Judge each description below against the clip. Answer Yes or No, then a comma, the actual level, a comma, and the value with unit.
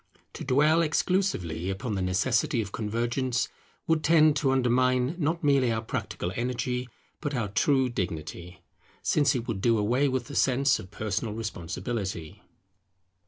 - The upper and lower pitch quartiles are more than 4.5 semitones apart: Yes, average, 4.9 semitones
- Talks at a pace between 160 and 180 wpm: No, average, 145 wpm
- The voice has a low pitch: Yes, low, 125 Hz